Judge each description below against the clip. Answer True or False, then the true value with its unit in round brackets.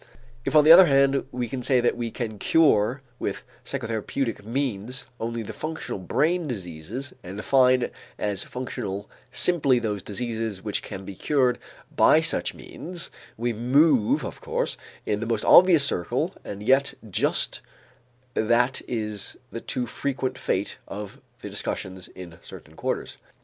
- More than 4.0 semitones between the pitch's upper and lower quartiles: True (4.6 semitones)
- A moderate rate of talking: True (145 wpm)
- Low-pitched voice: True (120 Hz)